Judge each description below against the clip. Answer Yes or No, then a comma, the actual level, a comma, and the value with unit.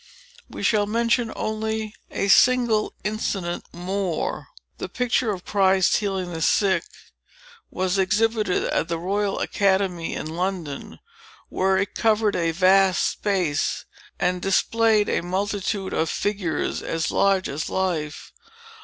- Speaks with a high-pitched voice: Yes, high, 195 Hz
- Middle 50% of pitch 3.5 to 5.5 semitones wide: No, average, 2.9 semitones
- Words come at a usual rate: No, slow, 125 wpm